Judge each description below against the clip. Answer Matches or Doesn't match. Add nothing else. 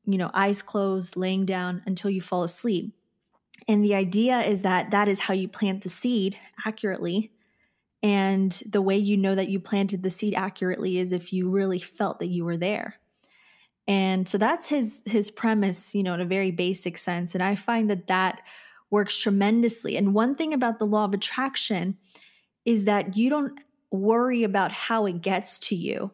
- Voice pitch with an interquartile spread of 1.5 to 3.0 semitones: Matches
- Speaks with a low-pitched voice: Doesn't match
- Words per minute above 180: Matches